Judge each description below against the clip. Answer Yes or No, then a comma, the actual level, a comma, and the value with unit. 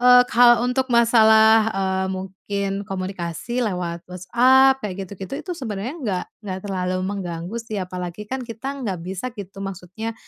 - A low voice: No, high, 200 Hz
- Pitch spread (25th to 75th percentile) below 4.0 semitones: No, average, 4.3 semitones